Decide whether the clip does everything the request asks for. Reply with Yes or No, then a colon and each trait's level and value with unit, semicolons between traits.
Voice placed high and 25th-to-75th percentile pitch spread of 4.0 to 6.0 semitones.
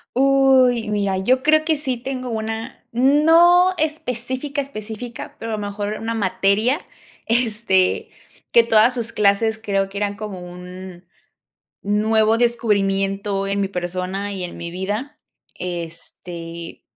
Yes: high, 215 Hz; average, 4.3 semitones